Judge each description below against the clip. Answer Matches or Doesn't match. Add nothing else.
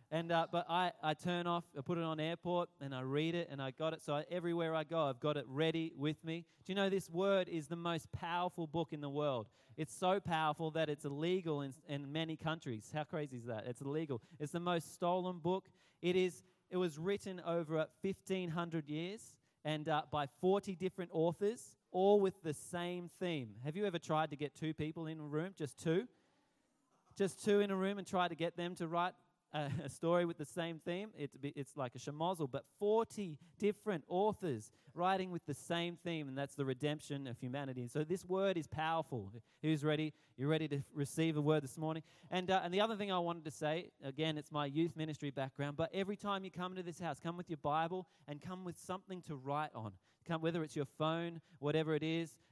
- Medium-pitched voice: Matches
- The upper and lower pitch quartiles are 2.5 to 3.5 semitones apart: Matches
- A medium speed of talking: Doesn't match